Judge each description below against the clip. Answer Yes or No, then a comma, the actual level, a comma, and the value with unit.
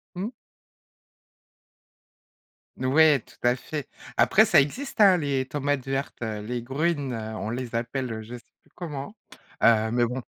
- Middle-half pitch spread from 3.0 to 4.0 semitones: Yes, average, 3.6 semitones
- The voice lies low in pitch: Yes, low, 130 Hz